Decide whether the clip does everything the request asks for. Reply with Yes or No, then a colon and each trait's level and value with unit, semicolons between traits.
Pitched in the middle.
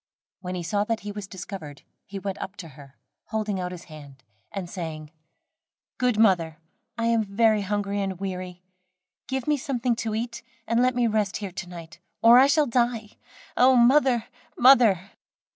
No: high, 205 Hz